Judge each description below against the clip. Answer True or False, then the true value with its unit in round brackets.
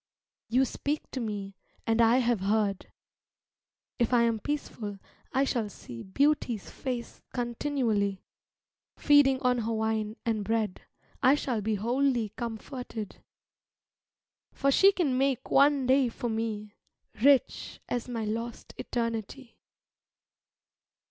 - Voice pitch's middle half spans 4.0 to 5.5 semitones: False (3.4 semitones)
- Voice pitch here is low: False (235 Hz)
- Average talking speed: False (120 wpm)